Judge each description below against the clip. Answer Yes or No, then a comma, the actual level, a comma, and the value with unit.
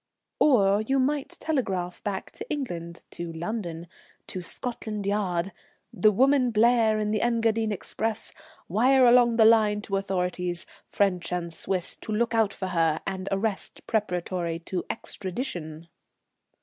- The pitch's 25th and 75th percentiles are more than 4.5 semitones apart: No, average, 4.2 semitones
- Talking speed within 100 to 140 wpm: Yes, slow, 135 wpm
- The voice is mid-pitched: No, high, 205 Hz